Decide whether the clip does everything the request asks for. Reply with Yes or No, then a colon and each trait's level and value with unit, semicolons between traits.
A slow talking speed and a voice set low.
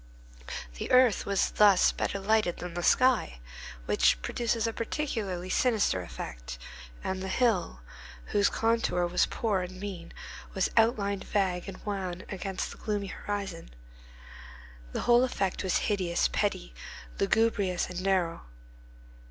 No: slow, 130 wpm; high, 195 Hz